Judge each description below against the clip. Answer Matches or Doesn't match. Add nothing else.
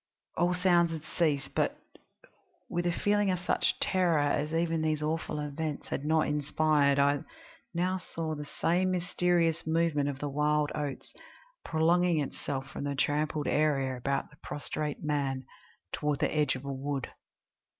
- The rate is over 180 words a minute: Doesn't match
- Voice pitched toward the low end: Doesn't match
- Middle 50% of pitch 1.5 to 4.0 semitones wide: Matches